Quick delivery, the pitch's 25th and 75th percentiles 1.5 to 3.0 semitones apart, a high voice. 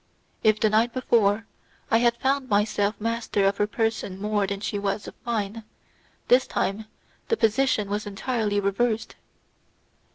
No: average, 150 wpm; narrow, 2.4 semitones; high, 215 Hz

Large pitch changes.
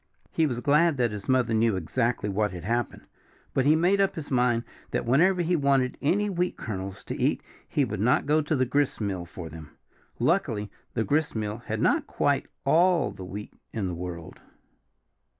Yes: wide, 6.6 semitones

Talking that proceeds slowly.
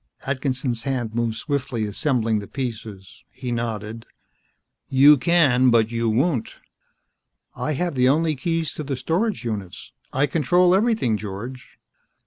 Yes: slow, 130 wpm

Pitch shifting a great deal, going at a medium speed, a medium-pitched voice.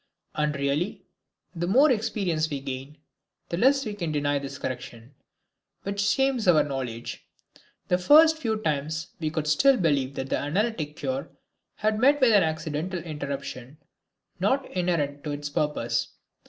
Yes: wide, 6.8 semitones; average, 150 wpm; medium, 155 Hz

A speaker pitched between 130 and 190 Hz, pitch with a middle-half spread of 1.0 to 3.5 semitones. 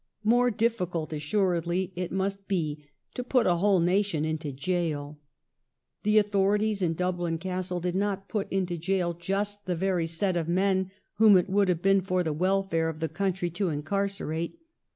Yes: medium, 185 Hz; average, 2.9 semitones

